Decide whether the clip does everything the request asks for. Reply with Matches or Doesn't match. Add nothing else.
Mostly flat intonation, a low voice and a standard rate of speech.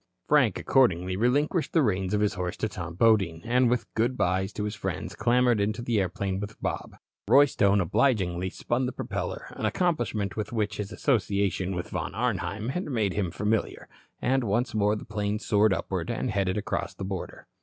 Doesn't match